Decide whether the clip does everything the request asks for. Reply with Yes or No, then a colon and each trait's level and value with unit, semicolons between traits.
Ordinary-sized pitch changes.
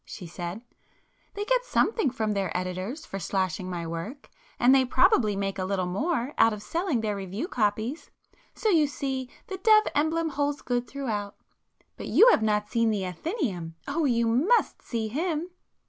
No: wide, 7.5 semitones